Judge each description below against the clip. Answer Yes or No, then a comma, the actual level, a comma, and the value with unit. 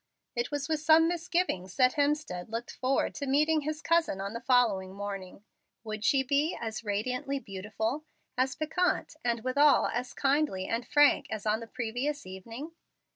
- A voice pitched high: Yes, very high, 255 Hz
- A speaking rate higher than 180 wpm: No, average, 165 wpm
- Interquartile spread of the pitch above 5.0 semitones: Yes, wide, 5.5 semitones